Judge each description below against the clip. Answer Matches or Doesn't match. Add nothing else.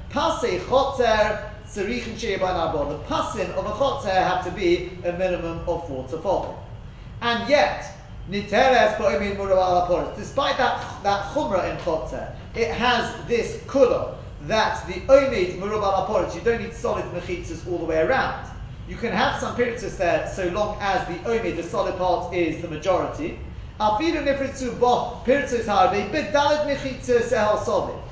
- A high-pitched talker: Matches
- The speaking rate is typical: Doesn't match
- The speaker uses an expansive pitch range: Matches